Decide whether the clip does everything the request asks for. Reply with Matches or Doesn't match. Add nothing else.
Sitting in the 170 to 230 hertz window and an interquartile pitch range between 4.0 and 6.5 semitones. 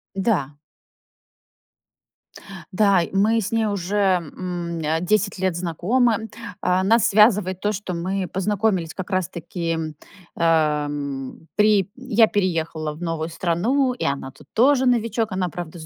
Matches